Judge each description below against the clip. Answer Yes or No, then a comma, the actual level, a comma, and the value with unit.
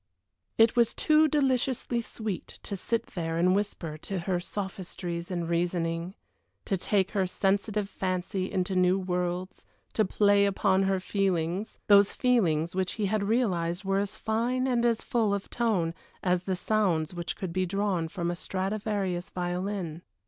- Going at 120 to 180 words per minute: Yes, average, 155 wpm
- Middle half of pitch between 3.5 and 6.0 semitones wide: No, average, 2.9 semitones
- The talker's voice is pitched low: No, high, 190 Hz